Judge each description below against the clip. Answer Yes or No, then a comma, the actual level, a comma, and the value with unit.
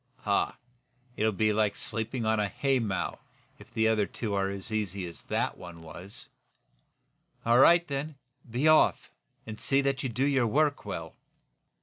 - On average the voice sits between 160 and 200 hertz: No, low, 110 Hz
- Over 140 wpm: Yes, average, 160 wpm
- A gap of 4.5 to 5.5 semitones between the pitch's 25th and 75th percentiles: Yes, average, 5.0 semitones